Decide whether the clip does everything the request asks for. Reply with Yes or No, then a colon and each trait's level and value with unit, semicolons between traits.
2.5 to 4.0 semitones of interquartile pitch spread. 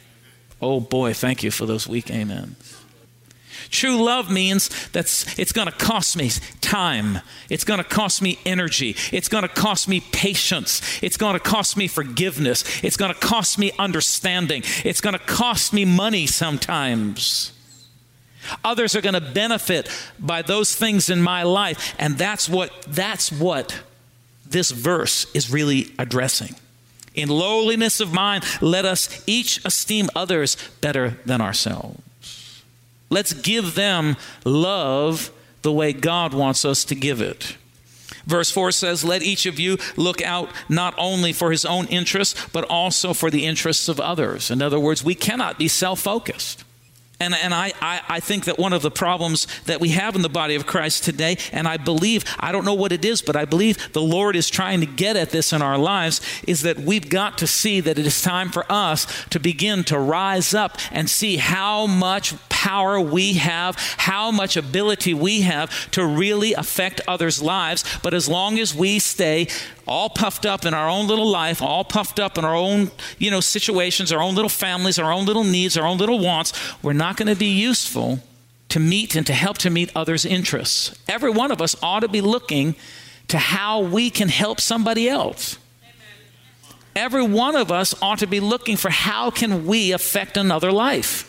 No: average, 5.1 semitones